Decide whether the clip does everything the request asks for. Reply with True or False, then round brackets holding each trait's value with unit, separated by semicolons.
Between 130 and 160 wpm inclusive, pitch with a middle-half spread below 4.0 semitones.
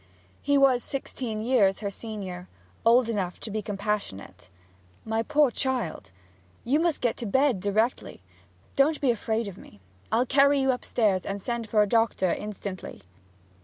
False (155 wpm; 4.3 semitones)